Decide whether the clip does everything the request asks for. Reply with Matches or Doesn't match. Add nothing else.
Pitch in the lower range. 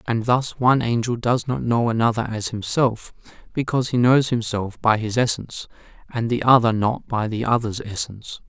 Matches